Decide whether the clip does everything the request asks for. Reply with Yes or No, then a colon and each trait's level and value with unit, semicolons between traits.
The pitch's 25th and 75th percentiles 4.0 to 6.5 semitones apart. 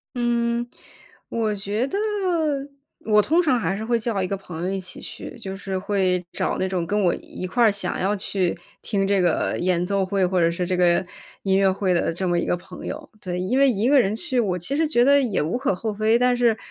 Yes: average, 4.3 semitones